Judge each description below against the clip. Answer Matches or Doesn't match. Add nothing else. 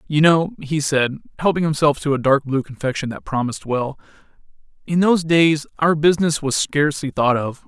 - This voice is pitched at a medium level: Matches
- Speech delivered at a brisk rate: Doesn't match